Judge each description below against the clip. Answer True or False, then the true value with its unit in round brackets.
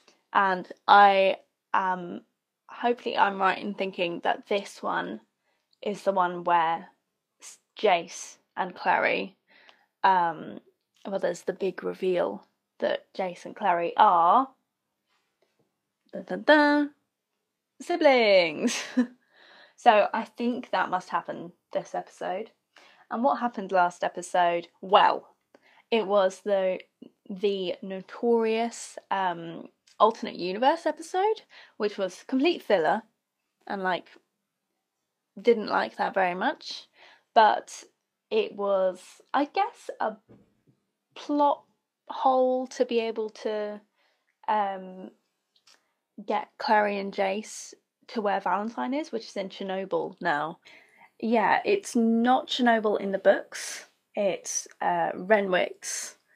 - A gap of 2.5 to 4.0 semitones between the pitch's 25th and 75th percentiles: False (5.1 semitones)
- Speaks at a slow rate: True (110 wpm)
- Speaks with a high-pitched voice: True (210 Hz)